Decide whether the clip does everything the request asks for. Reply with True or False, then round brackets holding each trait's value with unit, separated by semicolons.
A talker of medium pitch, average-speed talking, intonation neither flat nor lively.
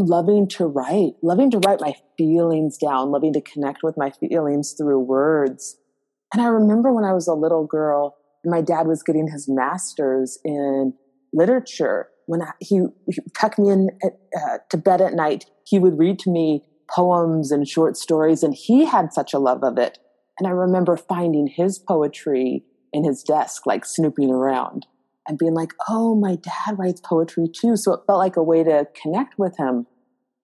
True (165 Hz; 185 wpm; 4.4 semitones)